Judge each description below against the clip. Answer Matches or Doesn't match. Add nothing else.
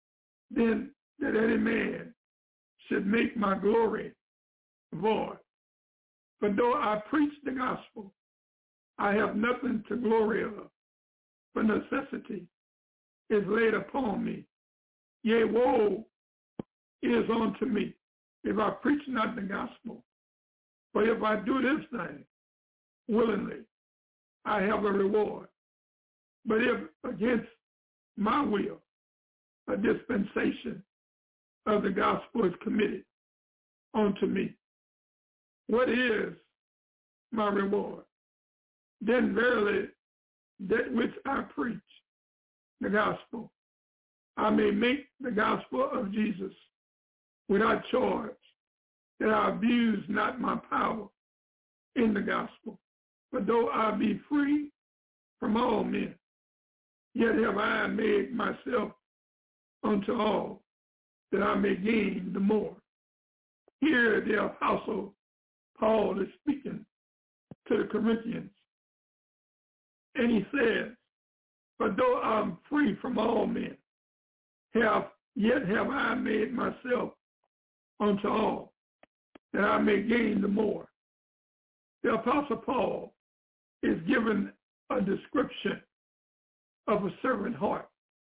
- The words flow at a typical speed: Doesn't match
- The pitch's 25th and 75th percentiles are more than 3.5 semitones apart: Doesn't match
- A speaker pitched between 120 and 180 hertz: Doesn't match